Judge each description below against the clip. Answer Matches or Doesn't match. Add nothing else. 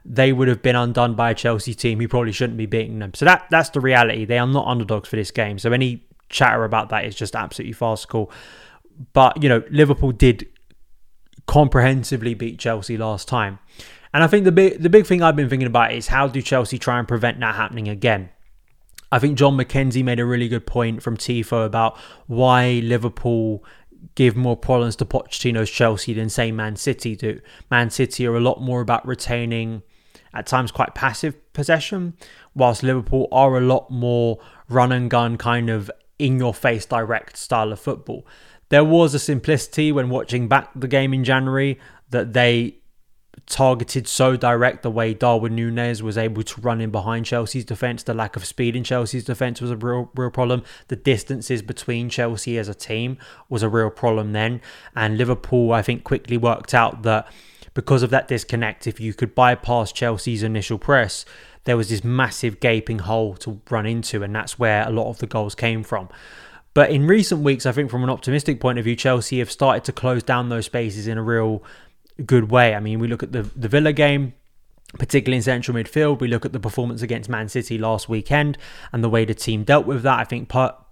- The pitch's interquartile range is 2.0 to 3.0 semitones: Matches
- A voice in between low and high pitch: Doesn't match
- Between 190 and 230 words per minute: Matches